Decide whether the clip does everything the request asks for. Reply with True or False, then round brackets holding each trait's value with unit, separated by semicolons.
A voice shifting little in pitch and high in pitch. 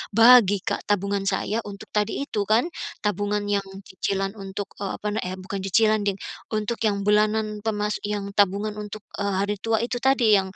True (1.3 semitones; 205 Hz)